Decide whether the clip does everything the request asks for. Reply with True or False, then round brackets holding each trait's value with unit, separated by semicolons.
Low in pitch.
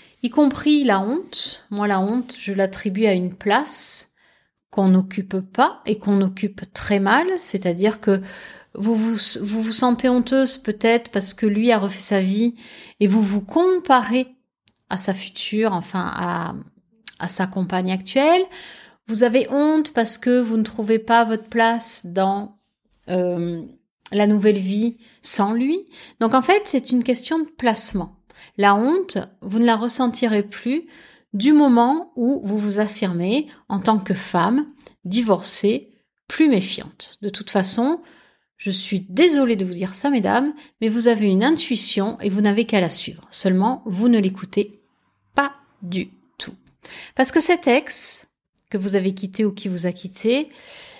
False (220 Hz)